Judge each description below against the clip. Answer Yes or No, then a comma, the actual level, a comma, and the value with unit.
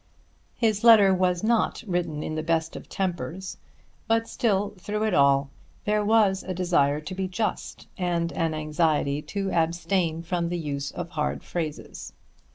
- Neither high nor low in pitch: Yes, medium, 175 Hz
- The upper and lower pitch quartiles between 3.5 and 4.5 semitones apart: Yes, average, 3.8 semitones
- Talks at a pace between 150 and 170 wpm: Yes, average, 160 wpm